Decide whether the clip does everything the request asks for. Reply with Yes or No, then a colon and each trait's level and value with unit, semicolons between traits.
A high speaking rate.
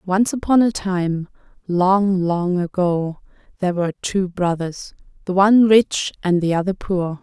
No: average, 150 wpm